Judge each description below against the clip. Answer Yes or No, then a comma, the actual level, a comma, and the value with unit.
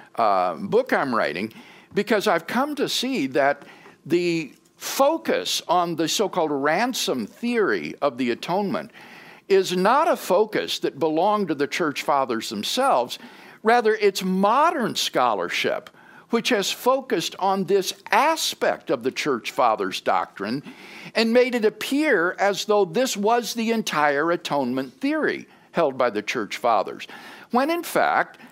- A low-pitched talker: No, high, 210 Hz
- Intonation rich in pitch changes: Yes, wide, 6.6 semitones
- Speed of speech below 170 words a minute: Yes, average, 140 wpm